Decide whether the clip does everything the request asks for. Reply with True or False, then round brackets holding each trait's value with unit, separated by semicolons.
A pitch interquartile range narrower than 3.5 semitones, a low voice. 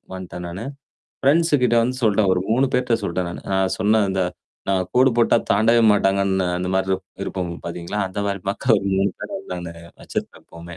False (3.9 semitones; 95 Hz)